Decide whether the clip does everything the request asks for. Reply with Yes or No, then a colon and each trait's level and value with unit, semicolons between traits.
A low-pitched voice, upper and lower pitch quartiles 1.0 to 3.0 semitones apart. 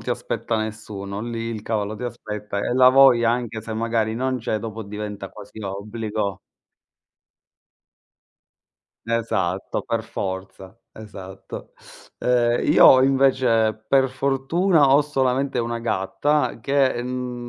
No: low, 115 Hz; average, 3.4 semitones